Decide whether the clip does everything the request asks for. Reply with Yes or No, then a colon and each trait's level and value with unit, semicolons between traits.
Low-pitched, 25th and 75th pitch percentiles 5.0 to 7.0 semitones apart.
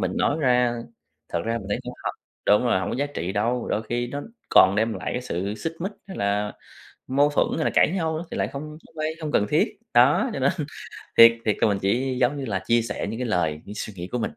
Yes: low, 120 Hz; wide, 5.6 semitones